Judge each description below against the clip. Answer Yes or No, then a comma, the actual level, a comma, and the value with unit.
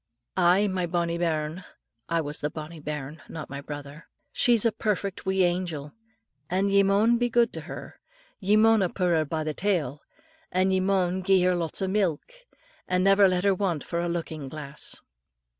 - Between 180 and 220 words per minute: Yes, average, 185 wpm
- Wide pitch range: No, average, 3.8 semitones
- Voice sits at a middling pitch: Yes, medium, 180 Hz